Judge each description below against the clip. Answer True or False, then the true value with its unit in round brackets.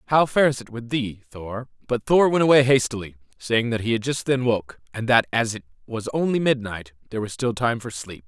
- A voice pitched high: False (120 Hz)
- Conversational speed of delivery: False (225 wpm)